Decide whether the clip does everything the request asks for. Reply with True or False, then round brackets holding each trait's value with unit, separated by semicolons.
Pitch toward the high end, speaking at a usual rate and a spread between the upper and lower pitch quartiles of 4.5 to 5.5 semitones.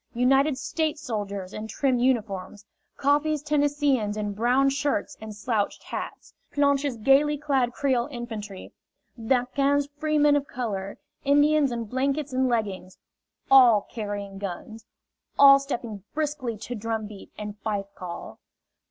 False (245 Hz; 125 wpm; 5.1 semitones)